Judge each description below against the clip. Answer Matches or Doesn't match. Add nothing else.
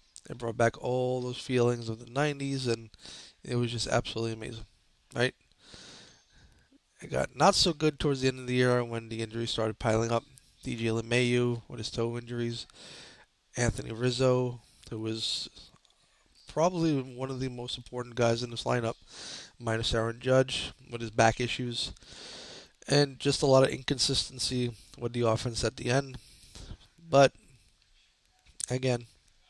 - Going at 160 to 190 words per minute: Doesn't match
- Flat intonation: Matches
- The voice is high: Doesn't match